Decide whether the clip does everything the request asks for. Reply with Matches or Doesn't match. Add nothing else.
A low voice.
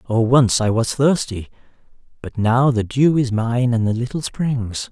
Matches